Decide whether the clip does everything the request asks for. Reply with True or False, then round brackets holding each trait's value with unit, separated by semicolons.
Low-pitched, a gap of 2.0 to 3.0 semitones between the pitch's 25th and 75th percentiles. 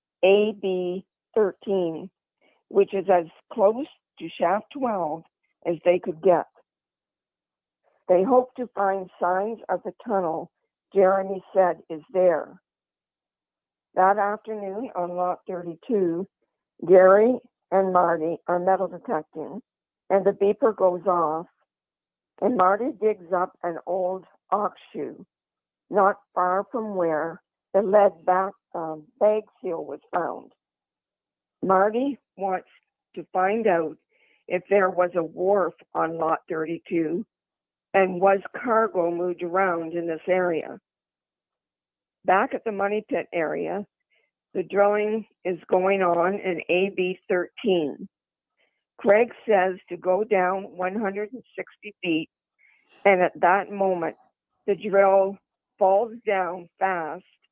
False (190 Hz; 2.4 semitones)